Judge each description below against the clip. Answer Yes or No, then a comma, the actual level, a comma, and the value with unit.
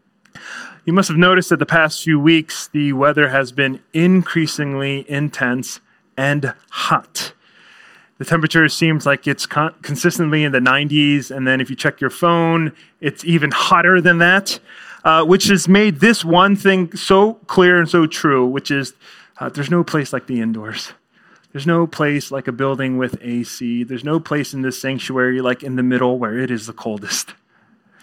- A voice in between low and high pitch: Yes, medium, 145 Hz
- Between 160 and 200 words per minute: Yes, average, 180 wpm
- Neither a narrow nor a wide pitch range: Yes, average, 4.2 semitones